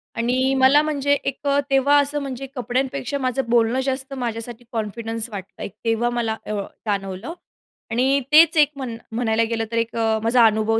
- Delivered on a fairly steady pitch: No, average, 3.2 semitones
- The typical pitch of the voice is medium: No, high, 245 Hz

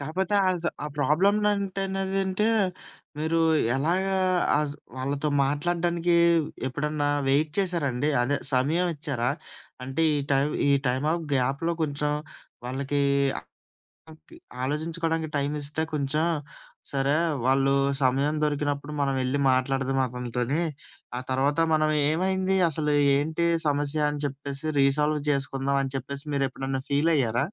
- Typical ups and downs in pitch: Yes, average, 3.2 semitones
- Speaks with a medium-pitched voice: Yes, medium, 145 Hz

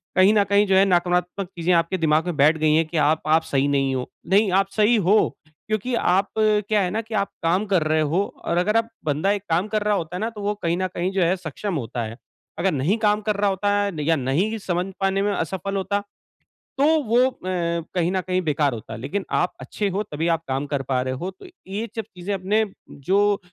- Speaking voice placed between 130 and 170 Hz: No, medium, 185 Hz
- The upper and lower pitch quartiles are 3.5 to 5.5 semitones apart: Yes, average, 4.2 semitones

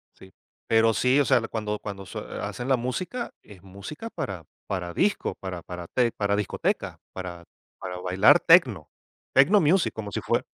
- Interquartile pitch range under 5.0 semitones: No, wide, 5.6 semitones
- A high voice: No, low, 105 Hz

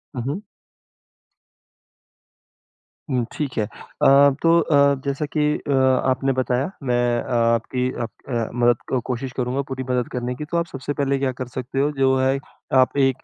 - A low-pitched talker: Yes, low, 130 Hz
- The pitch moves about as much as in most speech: No, narrow, 1.9 semitones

